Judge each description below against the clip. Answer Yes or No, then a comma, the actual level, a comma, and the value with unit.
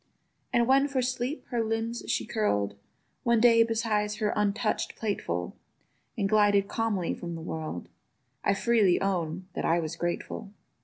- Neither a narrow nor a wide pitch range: Yes, average, 4.7 semitones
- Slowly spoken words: No, average, 150 wpm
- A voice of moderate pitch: No, high, 210 Hz